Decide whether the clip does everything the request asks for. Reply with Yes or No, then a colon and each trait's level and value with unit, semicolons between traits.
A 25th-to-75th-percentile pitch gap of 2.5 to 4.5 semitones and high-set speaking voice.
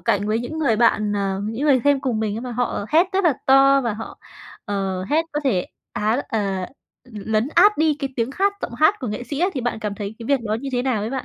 No: average, 4.9 semitones; high, 240 Hz